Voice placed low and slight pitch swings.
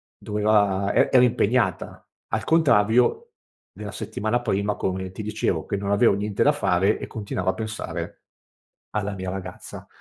Yes: low, 105 Hz; narrow, 2.2 semitones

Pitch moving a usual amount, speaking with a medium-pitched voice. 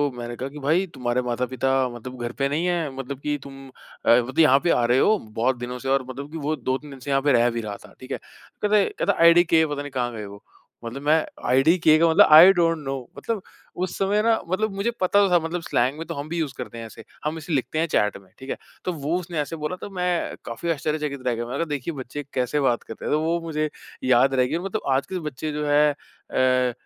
Yes: average, 4.5 semitones; medium, 145 Hz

